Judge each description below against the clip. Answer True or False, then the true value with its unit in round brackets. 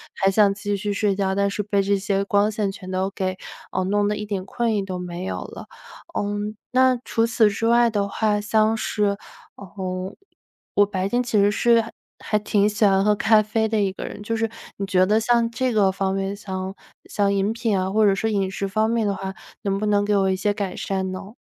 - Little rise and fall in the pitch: True (1.8 semitones)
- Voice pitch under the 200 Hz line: False (205 Hz)